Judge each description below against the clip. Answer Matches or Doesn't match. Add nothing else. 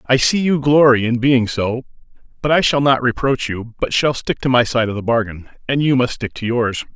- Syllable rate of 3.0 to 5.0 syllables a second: Doesn't match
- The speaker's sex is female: Doesn't match